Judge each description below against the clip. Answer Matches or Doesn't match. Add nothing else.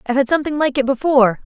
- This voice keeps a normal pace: Doesn't match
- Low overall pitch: Doesn't match